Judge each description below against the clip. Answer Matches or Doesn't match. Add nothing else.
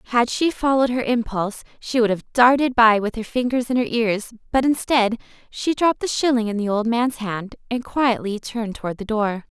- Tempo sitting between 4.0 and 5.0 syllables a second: Doesn't match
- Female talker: Matches